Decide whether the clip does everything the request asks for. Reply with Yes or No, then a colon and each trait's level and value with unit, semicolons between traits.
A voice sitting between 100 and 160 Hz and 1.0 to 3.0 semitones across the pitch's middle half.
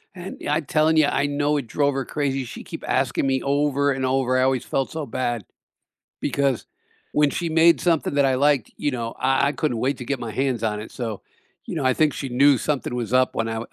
Yes: low, 135 Hz; narrow, 2.6 semitones